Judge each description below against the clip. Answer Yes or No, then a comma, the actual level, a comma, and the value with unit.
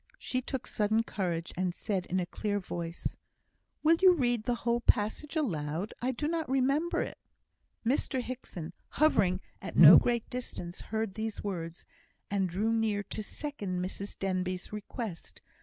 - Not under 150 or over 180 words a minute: Yes, average, 155 wpm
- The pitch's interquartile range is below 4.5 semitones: No, wide, 5.5 semitones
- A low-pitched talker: No, high, 210 Hz